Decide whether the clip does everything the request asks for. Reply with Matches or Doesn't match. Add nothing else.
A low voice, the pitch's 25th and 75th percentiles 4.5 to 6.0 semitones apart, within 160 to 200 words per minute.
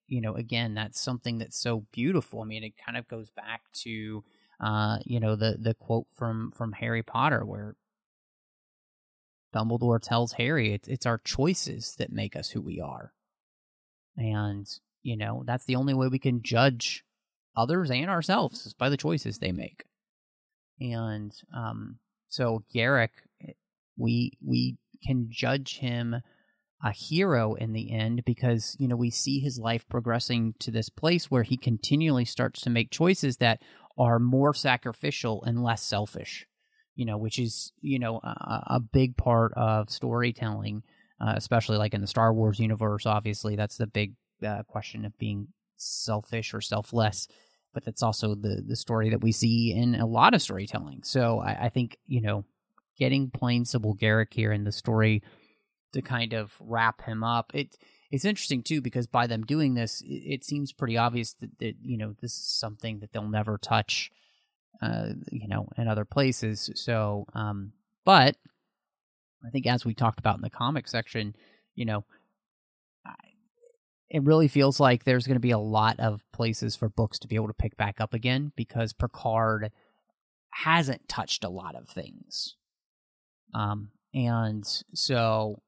Doesn't match